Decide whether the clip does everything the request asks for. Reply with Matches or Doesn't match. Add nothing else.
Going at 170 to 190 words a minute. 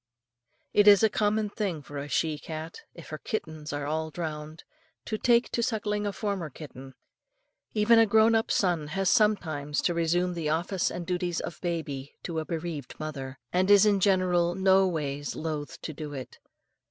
Matches